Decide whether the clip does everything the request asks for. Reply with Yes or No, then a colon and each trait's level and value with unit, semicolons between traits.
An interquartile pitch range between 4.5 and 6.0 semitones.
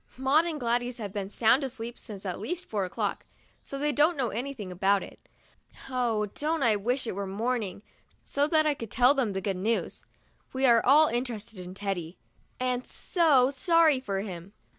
Yes: average, 5.3 semitones